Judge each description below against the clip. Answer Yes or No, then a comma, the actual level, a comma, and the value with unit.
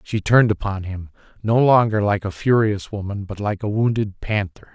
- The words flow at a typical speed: Yes, average, 190 wpm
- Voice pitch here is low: Yes, low, 105 Hz